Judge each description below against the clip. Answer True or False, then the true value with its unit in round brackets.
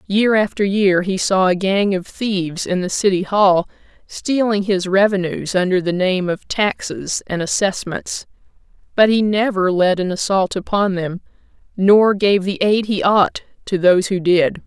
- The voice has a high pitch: True (195 Hz)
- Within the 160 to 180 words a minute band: True (170 wpm)